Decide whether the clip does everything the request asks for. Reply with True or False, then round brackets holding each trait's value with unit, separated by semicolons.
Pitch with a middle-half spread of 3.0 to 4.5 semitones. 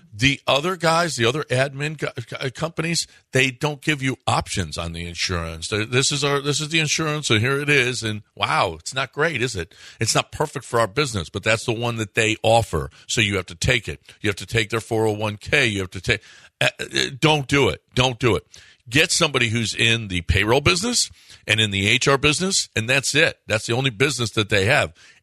False (5.4 semitones)